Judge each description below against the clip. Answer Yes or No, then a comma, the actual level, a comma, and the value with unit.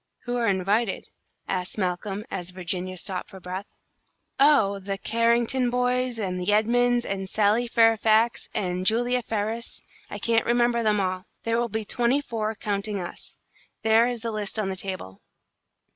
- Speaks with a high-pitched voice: Yes, high, 215 Hz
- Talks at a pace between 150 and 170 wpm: Yes, average, 160 wpm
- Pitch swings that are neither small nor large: Yes, average, 3.6 semitones